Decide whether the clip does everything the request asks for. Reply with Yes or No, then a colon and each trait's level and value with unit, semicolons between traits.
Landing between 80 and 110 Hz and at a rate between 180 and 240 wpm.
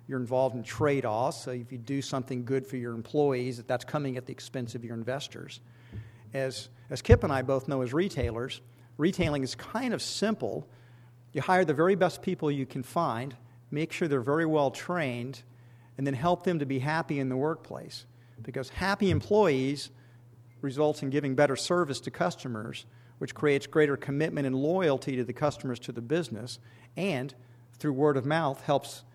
No: low, 135 Hz; average, 185 wpm